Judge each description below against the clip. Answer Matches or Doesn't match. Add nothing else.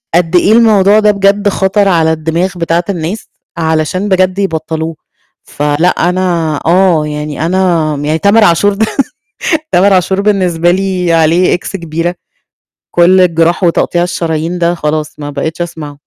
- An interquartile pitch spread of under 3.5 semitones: Matches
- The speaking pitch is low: Doesn't match